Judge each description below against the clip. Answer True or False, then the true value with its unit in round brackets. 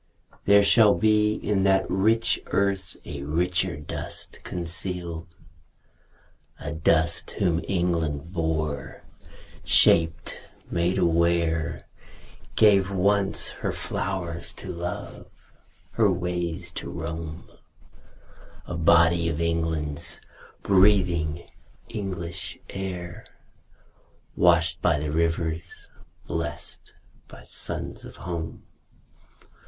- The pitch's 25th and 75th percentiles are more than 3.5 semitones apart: False (2.6 semitones)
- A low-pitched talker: True (85 Hz)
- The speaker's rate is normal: False (90 wpm)